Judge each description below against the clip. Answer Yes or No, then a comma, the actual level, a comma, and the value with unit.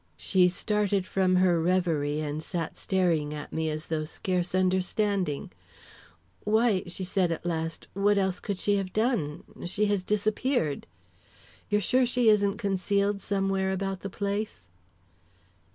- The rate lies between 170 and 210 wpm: No, average, 145 wpm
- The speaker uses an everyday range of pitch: Yes, average, 3.0 semitones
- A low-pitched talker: No, high, 190 Hz